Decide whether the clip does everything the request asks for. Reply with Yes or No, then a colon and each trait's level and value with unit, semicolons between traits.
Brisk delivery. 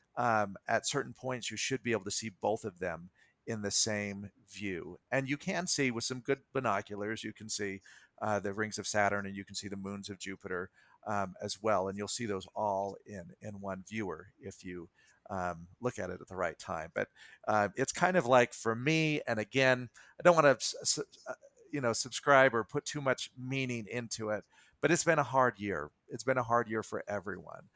Yes: fast, 215 wpm